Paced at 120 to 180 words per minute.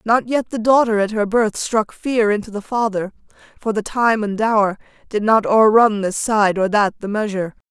No: average, 200 wpm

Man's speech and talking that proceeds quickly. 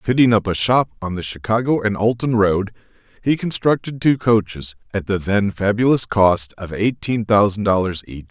No: male; average, 175 wpm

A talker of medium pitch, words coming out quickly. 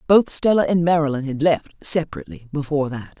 No: medium, 150 Hz; average, 170 wpm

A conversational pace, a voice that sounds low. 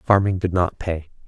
Yes: average, 190 wpm; very low, 90 Hz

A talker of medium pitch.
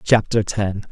No: low, 105 Hz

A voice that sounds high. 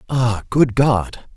No: low, 120 Hz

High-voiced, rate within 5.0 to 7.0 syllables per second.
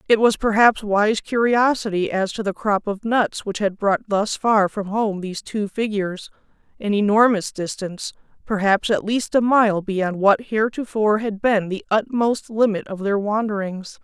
No: high, 210 Hz; 4.7 syllables/s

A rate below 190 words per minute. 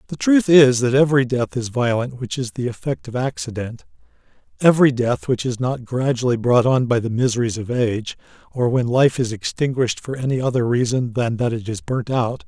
No: average, 200 wpm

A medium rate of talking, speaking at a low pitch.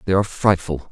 Yes: average, 195 wpm; very low, 90 Hz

